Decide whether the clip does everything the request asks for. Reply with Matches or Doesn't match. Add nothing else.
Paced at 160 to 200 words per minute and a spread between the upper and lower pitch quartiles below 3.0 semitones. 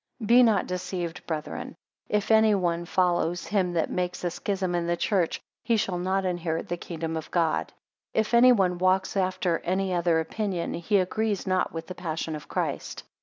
Matches